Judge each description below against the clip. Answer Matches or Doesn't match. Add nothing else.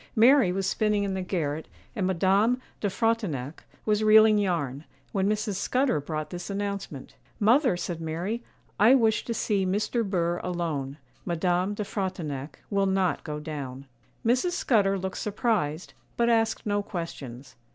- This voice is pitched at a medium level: Doesn't match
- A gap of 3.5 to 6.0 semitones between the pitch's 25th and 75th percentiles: Matches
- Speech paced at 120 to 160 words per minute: Matches